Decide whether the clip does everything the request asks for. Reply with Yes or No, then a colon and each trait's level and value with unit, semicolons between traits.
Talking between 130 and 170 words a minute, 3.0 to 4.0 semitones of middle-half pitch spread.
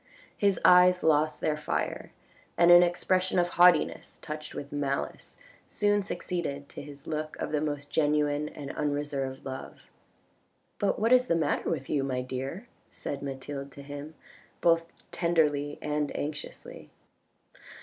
Yes: average, 145 wpm; average, 3.3 semitones